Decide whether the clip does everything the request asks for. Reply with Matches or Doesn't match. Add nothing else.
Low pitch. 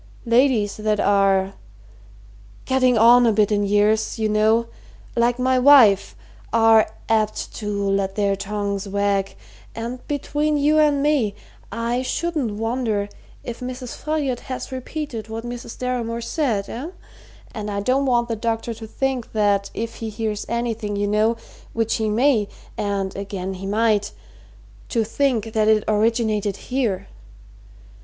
Doesn't match